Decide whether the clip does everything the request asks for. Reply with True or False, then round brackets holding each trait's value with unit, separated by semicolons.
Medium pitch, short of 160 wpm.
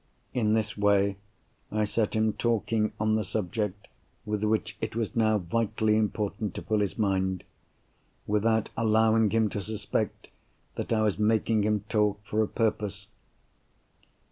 False (105 Hz; 145 wpm)